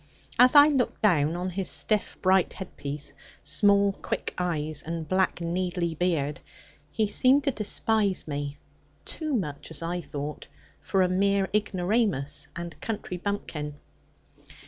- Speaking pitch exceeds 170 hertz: Yes, medium, 185 Hz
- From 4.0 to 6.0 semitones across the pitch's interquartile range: Yes, average, 4.6 semitones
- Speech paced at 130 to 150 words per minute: Yes, average, 140 wpm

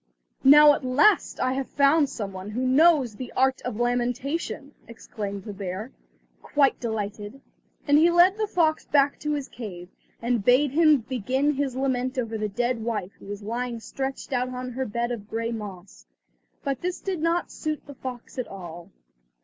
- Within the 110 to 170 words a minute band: No, average, 180 wpm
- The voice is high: Yes, very high, 255 Hz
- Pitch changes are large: No, average, 4.4 semitones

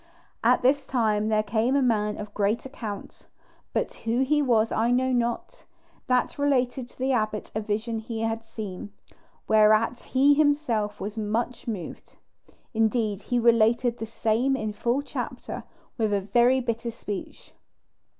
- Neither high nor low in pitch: No, high, 230 Hz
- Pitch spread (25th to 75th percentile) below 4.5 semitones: Yes, average, 2.7 semitones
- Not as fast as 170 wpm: Yes, average, 150 wpm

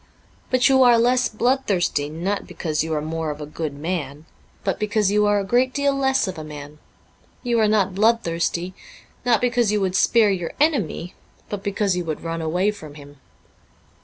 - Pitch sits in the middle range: No, high, 195 Hz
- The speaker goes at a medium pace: Yes, average, 190 wpm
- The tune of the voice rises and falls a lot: Yes, wide, 6.2 semitones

